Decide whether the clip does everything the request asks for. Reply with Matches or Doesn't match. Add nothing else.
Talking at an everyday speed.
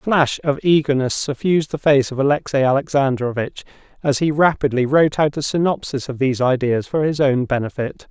Matches